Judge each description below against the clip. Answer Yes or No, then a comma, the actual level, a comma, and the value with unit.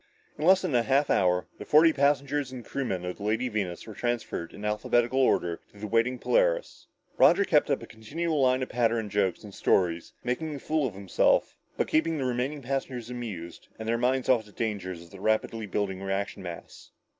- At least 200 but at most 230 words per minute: Yes, fast, 205 wpm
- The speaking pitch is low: Yes, low, 120 Hz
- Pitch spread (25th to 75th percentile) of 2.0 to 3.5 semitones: No, average, 5.2 semitones